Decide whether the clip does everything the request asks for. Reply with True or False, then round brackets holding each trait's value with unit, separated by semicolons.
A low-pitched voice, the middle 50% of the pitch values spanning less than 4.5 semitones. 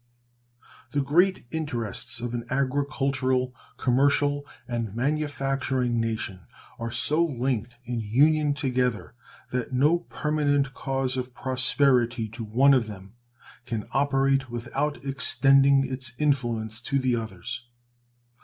True (130 Hz; 2.8 semitones)